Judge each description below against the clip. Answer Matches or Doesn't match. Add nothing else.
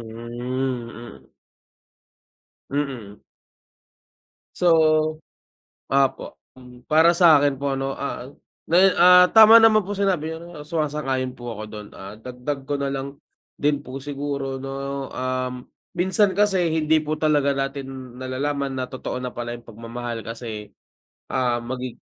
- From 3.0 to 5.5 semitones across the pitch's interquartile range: Matches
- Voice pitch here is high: Doesn't match